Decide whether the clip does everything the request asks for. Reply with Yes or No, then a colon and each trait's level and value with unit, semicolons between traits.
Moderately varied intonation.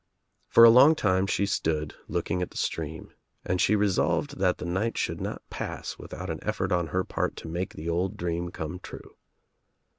Yes: average, 3.0 semitones